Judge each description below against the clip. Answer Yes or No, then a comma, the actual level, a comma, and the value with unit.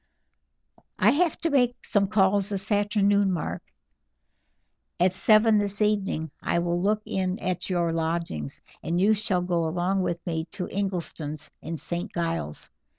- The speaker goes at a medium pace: Yes, average, 150 wpm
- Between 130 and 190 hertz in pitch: Yes, medium, 185 Hz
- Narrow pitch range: No, average, 3.2 semitones